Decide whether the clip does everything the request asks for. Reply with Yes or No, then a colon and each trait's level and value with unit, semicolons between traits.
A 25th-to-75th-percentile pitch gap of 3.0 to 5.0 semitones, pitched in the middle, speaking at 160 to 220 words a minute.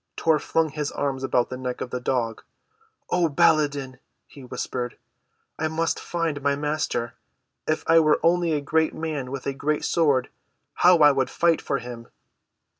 Yes: average, 3.5 semitones; medium, 145 Hz; average, 170 wpm